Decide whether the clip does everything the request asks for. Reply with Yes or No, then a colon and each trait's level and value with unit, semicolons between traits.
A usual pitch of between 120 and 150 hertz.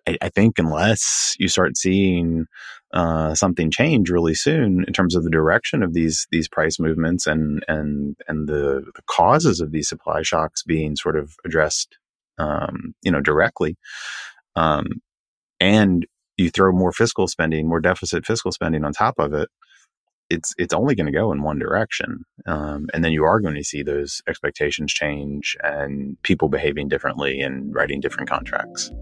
No: very low, 80 Hz